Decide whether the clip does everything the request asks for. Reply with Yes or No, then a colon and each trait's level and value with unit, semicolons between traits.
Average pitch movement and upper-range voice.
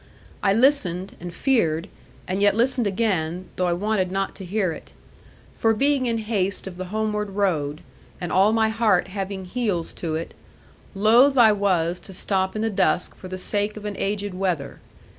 Yes: average, 3.1 semitones; high, 195 Hz